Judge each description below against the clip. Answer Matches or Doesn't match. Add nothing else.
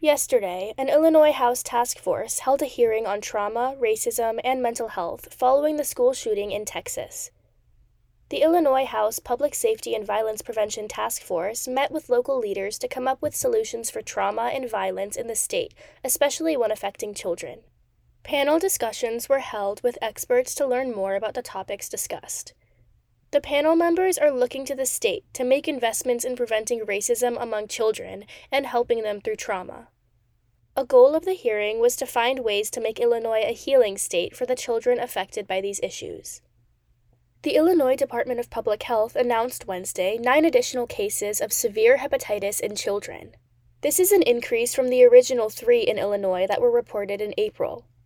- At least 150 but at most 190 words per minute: Matches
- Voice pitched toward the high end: Matches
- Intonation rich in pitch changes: Matches